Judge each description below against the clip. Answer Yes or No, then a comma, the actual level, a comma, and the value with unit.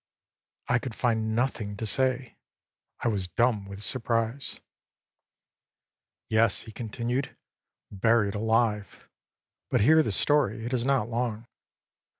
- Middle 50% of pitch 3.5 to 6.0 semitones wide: No, average, 2.7 semitones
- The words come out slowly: Yes, slow, 125 wpm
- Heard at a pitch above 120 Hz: No, low, 115 Hz